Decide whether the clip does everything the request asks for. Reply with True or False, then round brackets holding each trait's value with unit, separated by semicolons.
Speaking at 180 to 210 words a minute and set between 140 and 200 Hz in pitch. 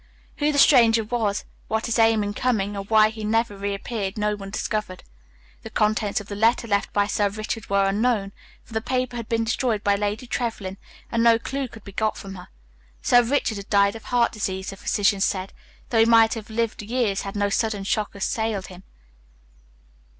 False (200 wpm; 215 Hz)